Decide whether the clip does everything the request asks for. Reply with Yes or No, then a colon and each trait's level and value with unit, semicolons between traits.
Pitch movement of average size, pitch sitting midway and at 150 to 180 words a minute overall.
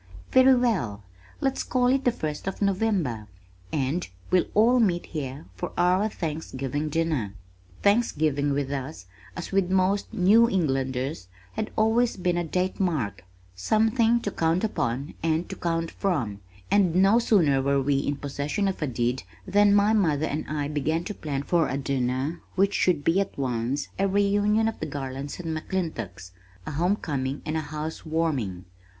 No: wide, 6.2 semitones; medium, 160 Hz; average, 160 wpm